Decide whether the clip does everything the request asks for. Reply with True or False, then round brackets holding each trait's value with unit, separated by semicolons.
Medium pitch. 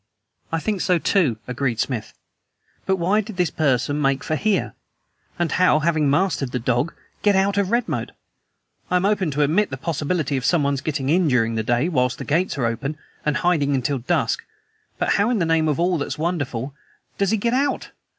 True (155 Hz)